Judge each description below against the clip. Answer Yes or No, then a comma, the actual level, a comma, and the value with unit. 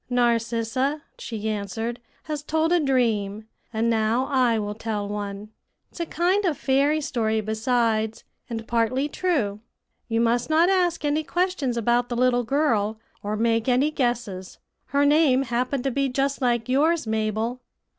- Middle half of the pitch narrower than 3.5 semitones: No, average, 4.3 semitones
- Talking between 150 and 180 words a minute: Yes, average, 155 wpm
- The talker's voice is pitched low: No, high, 240 Hz